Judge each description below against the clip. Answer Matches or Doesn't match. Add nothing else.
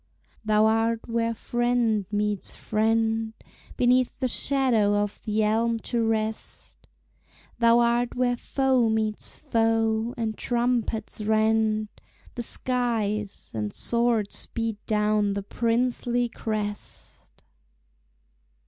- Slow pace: Matches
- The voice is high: Matches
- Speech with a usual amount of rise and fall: Doesn't match